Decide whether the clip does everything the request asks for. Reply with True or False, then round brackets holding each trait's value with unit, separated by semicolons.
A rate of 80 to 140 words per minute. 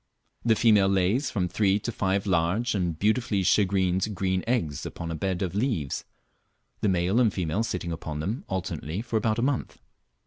False (175 wpm)